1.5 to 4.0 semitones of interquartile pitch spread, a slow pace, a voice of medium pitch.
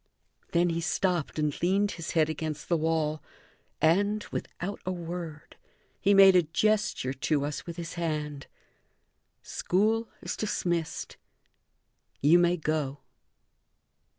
Yes: average, 3.2 semitones; slow, 125 wpm; medium, 170 Hz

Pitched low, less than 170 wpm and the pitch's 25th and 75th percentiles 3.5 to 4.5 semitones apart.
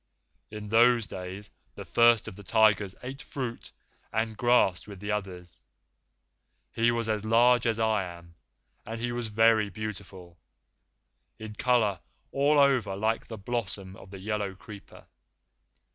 No: low, 110 Hz; average, 145 wpm; average, 3.0 semitones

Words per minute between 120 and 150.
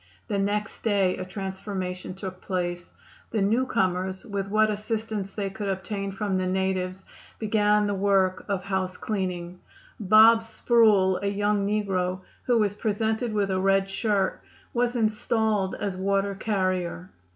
Yes: average, 140 wpm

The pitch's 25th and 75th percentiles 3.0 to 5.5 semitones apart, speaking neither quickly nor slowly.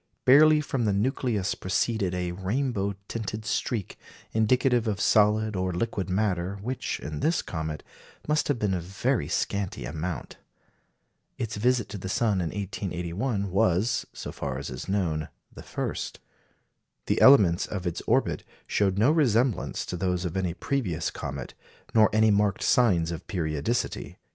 Yes: average, 4.5 semitones; average, 150 wpm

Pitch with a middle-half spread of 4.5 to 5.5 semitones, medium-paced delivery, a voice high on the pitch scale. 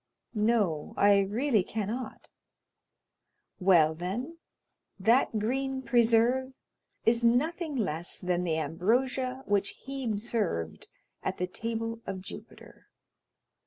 No: average, 5.2 semitones; slow, 100 wpm; high, 225 Hz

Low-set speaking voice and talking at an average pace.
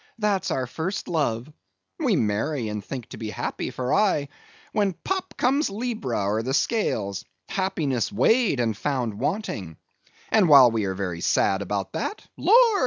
Yes: low, 130 Hz; average, 155 wpm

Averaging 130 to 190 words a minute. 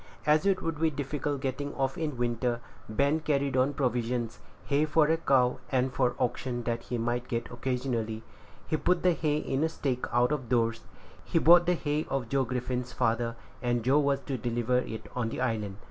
No: average, 200 wpm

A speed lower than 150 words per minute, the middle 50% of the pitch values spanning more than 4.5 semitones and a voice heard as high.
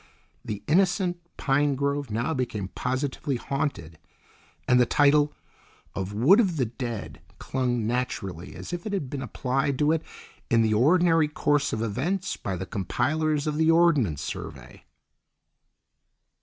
No: average, 140 wpm; average, 5.3 semitones; low, 135 Hz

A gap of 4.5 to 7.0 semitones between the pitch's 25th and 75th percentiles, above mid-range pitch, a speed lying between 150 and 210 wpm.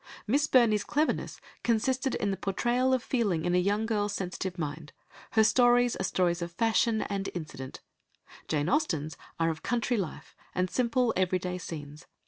Yes: wide, 5.6 semitones; high, 200 Hz; average, 160 wpm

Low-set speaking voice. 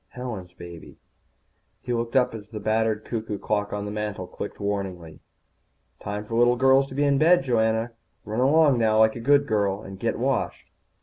Yes: low, 110 Hz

